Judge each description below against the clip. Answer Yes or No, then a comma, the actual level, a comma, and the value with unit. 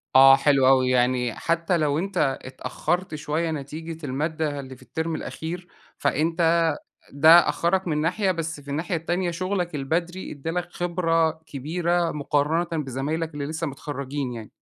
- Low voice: No, medium, 160 Hz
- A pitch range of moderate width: Yes, average, 3.2 semitones